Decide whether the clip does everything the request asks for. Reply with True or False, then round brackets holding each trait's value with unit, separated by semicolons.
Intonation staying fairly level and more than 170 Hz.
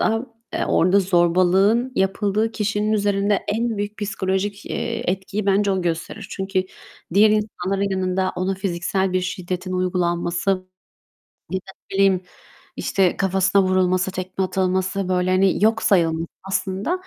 True (1.7 semitones; 190 Hz)